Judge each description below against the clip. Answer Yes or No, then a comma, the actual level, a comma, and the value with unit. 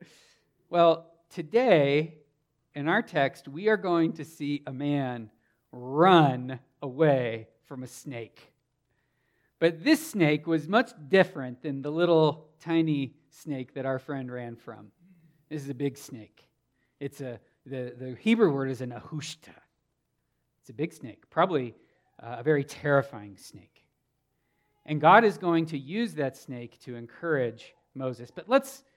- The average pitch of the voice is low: No, medium, 145 Hz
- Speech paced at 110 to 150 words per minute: Yes, average, 145 wpm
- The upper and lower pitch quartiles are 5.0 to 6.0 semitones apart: No, average, 4.3 semitones